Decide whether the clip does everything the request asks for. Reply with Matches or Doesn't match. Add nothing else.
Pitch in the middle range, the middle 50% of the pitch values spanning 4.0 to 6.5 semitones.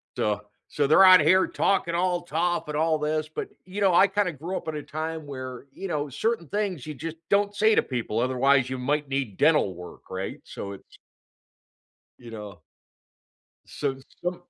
Matches